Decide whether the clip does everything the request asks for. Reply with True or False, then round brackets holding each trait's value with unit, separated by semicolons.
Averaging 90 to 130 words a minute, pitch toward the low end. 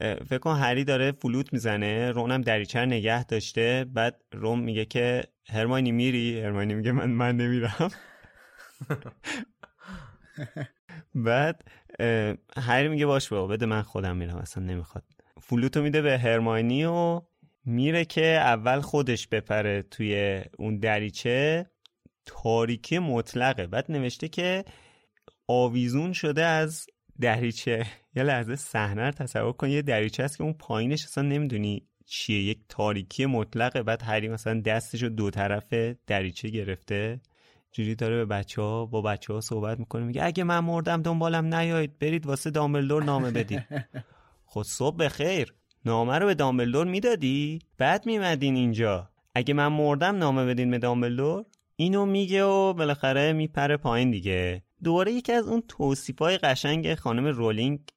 False (145 wpm; 125 Hz)